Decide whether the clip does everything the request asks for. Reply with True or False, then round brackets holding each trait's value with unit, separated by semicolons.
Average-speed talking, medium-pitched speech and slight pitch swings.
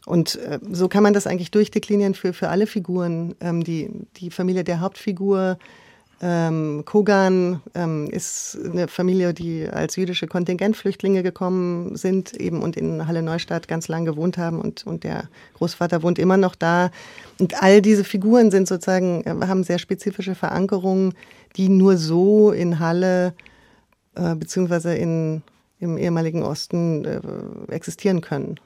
True (150 wpm; 180 Hz; 2.3 semitones)